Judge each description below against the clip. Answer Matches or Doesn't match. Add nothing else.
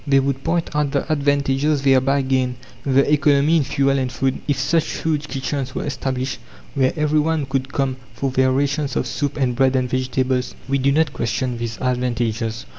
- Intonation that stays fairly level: Matches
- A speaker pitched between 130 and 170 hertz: Matches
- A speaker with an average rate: Matches